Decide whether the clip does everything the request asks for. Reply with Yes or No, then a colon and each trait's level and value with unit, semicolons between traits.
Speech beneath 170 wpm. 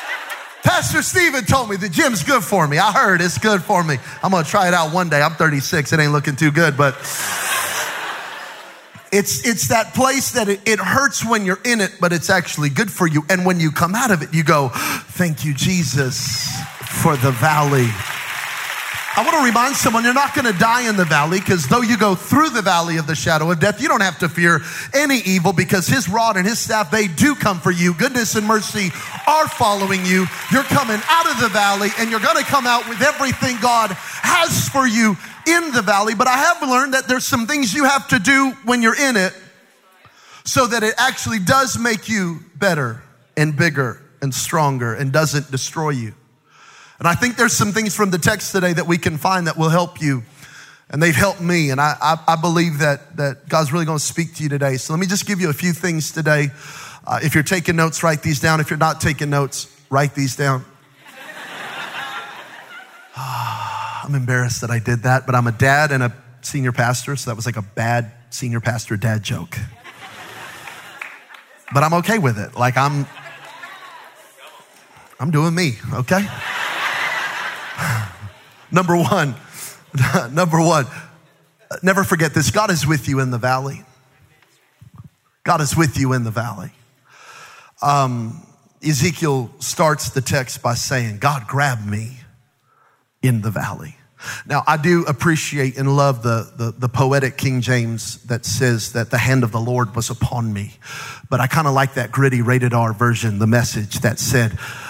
No: average, 190 wpm